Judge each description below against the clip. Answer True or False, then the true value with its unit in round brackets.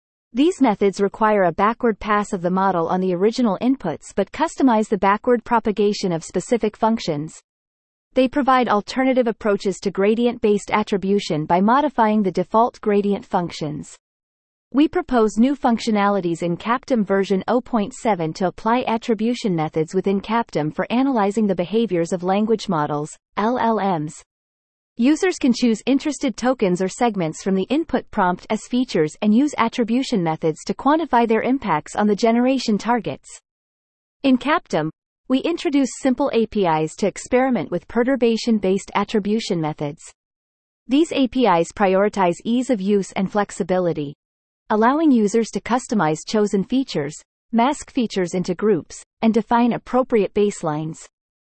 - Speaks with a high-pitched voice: True (215 Hz)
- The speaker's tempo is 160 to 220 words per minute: False (135 wpm)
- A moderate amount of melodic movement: True (4.6 semitones)